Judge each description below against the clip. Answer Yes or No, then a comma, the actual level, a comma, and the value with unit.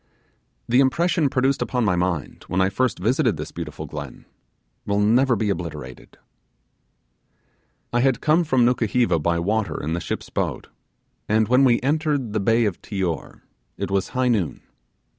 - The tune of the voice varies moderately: No, wide, 6.1 semitones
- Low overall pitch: Yes, low, 110 Hz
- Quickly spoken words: No, average, 160 wpm